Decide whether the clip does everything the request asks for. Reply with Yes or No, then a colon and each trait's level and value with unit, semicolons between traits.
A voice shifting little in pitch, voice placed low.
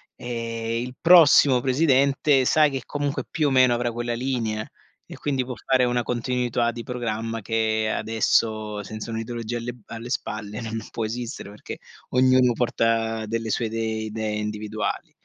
Yes: narrow, 2.3 semitones; low, 115 Hz